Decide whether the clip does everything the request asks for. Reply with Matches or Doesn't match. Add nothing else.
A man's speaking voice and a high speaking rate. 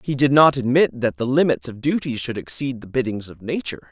Matches